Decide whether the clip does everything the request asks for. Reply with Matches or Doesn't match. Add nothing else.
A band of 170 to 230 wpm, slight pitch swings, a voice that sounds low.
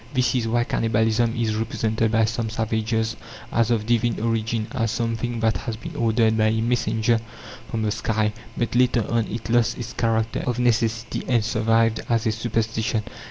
Matches